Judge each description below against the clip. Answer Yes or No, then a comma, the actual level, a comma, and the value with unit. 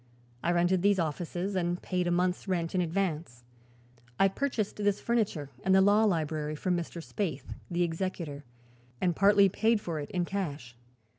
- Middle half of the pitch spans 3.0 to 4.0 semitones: Yes, average, 3.3 semitones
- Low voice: No, medium, 180 Hz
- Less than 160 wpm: No, average, 165 wpm